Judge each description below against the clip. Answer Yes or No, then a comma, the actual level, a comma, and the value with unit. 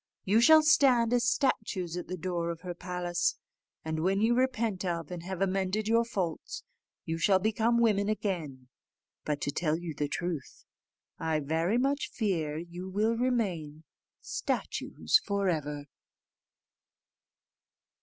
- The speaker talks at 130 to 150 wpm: Yes, average, 140 wpm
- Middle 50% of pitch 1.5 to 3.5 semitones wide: No, average, 5.2 semitones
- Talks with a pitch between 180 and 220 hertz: Yes, medium, 185 Hz